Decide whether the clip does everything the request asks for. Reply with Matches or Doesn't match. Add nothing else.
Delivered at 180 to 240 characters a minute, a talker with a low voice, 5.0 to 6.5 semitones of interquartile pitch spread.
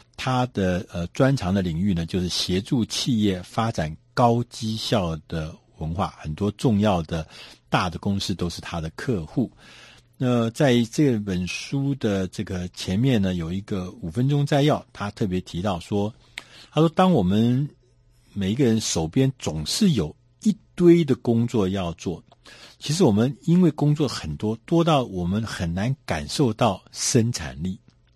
Matches